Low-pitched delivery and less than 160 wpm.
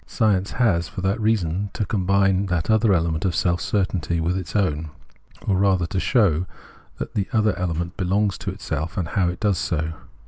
No: very low, 95 Hz; average, 185 wpm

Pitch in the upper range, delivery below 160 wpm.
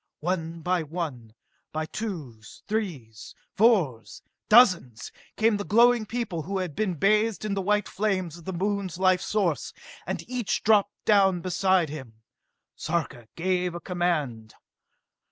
No: medium, 180 Hz; average, 140 wpm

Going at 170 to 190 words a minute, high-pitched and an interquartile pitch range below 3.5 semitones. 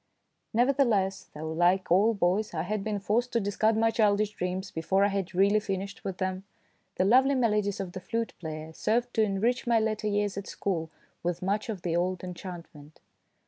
Yes: average, 185 wpm; high, 200 Hz; average, 3.1 semitones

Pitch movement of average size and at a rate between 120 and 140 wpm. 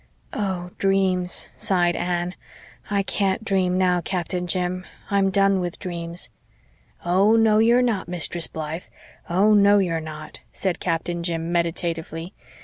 No: narrow, 2.3 semitones; slow, 135 wpm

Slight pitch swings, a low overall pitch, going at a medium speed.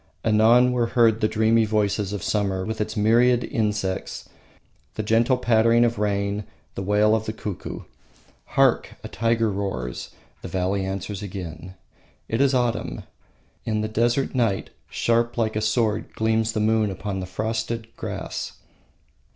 Yes: narrow, 2.3 semitones; low, 110 Hz; average, 150 wpm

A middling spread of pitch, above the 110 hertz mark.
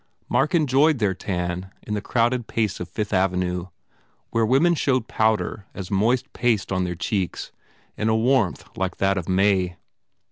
No: average, 4.4 semitones; low, 105 Hz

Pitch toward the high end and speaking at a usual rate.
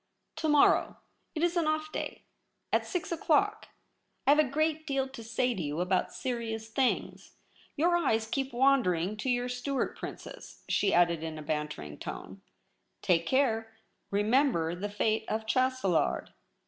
Yes: high, 240 Hz; average, 165 wpm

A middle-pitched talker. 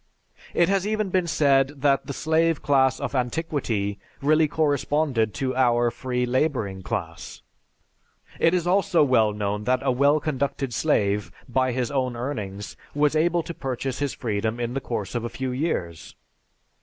No: low, 130 Hz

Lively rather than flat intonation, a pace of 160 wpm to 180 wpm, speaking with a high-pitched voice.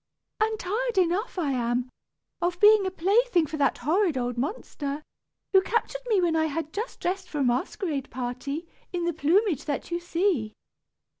Yes: wide, 5.7 semitones; average, 170 wpm; very high, 340 Hz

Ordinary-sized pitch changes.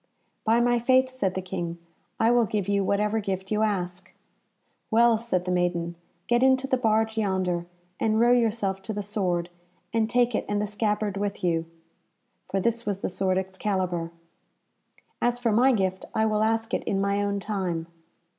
Yes: average, 3.2 semitones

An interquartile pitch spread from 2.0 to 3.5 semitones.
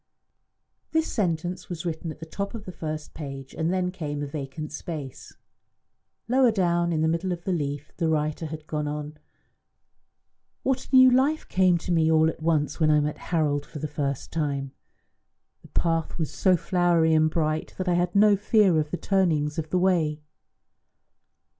Yes: average, 3.0 semitones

